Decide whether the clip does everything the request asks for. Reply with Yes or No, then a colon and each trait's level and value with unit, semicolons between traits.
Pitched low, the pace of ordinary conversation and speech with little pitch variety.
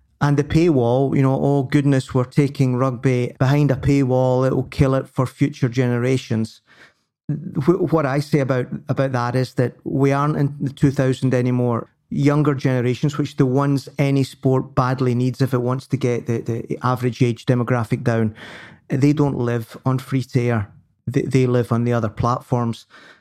Yes: low, 130 Hz; average, 175 wpm; narrow, 2.3 semitones